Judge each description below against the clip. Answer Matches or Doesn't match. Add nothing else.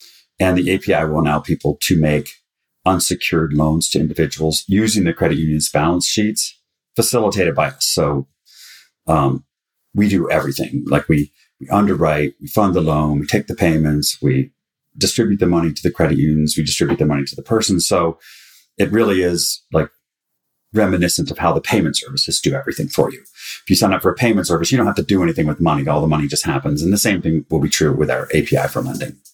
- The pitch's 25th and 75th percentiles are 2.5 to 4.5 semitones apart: Matches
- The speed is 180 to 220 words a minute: Matches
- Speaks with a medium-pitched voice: Doesn't match